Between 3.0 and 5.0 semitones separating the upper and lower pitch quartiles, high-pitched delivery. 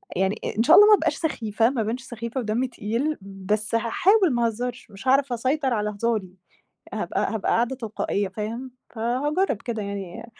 Yes: average, 3.5 semitones; high, 230 Hz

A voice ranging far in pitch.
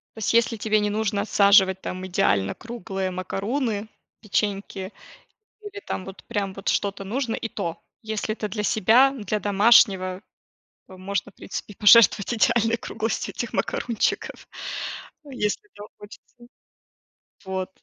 No: average, 2.8 semitones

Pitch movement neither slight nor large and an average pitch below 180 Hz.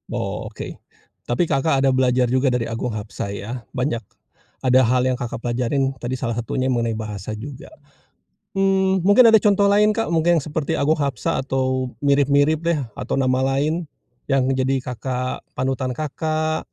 Yes: average, 3.9 semitones; low, 135 Hz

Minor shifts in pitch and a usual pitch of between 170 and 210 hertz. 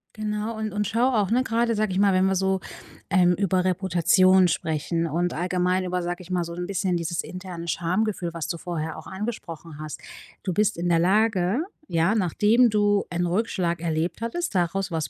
No: average, 3.4 semitones; medium, 185 Hz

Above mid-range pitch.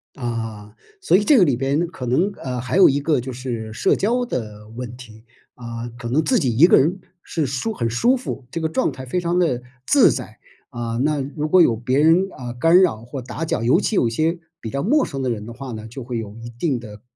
No: low, 130 Hz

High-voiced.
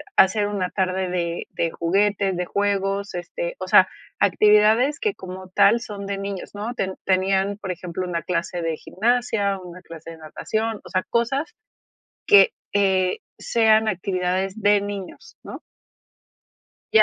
Yes: high, 195 Hz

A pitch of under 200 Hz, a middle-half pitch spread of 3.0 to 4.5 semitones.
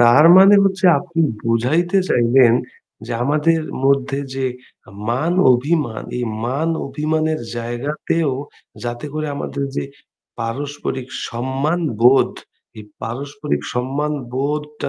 Yes: medium, 140 Hz; average, 3.9 semitones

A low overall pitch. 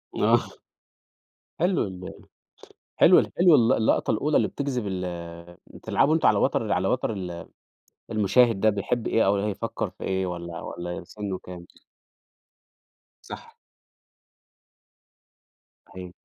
Yes: low, 100 Hz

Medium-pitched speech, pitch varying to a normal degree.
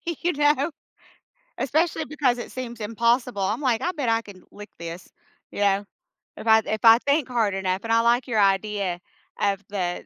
No: high, 225 Hz; average, 4.4 semitones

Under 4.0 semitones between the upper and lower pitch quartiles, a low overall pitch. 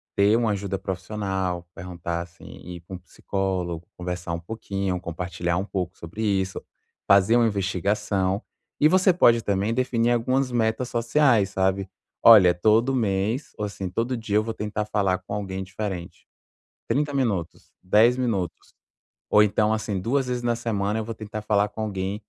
Yes: average, 3.4 semitones; low, 100 Hz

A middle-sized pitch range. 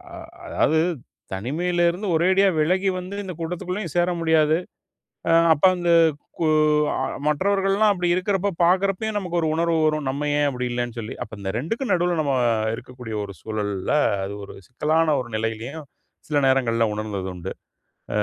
No: wide, 6.8 semitones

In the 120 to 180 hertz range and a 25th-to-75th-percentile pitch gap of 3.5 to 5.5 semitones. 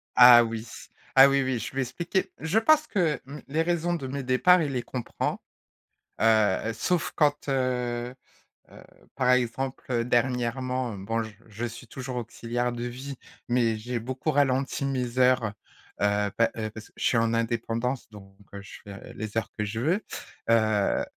No: low, 125 Hz; average, 3.0 semitones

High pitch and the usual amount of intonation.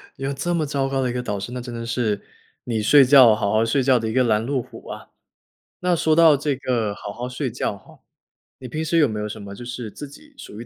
No: low, 125 Hz; average, 4.1 semitones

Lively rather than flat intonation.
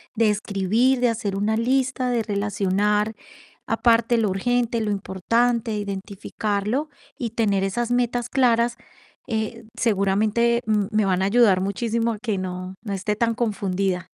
No: average, 3.0 semitones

